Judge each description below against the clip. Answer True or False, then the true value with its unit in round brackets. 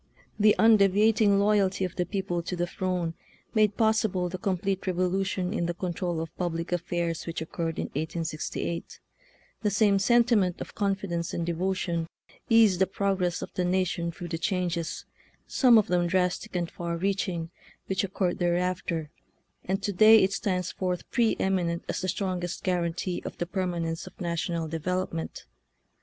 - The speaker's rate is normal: True (170 wpm)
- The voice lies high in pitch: False (180 Hz)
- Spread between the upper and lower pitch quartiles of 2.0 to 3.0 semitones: True (2.4 semitones)